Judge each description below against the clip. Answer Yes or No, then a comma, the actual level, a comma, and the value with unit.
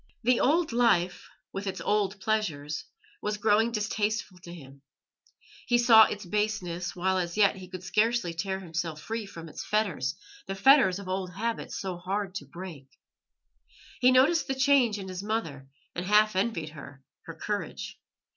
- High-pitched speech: Yes, high, 195 Hz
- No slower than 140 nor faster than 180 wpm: Yes, average, 165 wpm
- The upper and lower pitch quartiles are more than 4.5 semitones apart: No, average, 3.8 semitones